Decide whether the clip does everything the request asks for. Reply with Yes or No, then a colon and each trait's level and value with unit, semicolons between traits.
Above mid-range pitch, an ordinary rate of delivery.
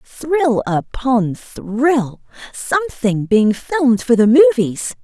No: very high, 250 Hz; slow, 105 wpm